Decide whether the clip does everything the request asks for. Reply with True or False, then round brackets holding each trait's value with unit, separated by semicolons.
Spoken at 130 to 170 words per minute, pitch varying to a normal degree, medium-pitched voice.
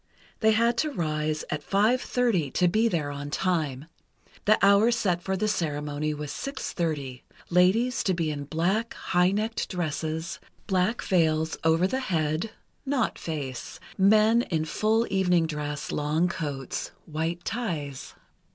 False (140 wpm; 5.8 semitones; 175 Hz)